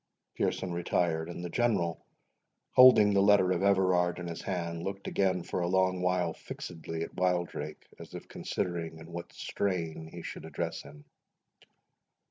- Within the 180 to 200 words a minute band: No, average, 155 wpm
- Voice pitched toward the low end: Yes, very low, 90 Hz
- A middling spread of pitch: No, narrow, 1.9 semitones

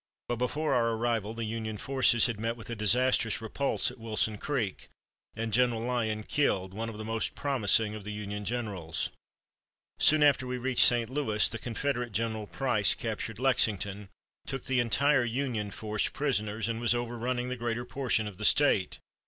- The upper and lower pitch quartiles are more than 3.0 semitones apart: No, narrow, 2.6 semitones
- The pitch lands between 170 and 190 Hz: No, low, 115 Hz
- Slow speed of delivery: No, average, 175 wpm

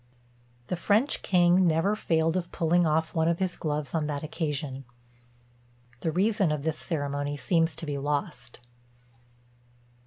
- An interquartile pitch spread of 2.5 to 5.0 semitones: Yes, average, 2.9 semitones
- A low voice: No, medium, 160 Hz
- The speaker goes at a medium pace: Yes, average, 145 wpm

